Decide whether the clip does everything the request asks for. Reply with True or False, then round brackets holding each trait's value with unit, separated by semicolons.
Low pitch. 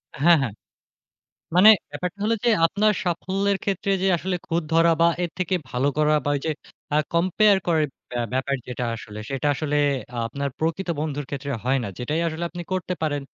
False (160 Hz)